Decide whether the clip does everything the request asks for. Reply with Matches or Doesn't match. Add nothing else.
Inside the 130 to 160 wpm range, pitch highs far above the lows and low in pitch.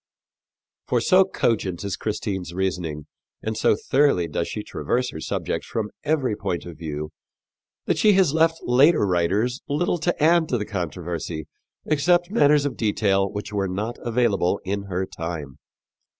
Matches